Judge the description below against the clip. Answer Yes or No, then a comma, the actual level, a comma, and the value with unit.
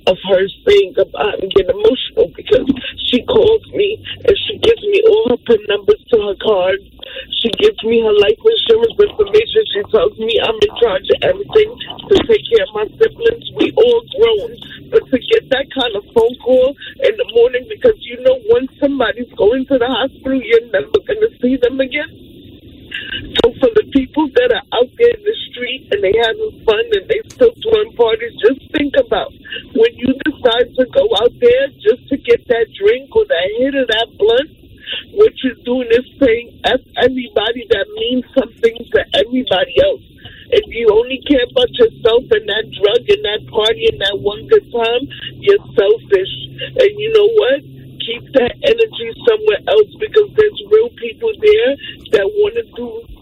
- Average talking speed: Yes, average, 185 wpm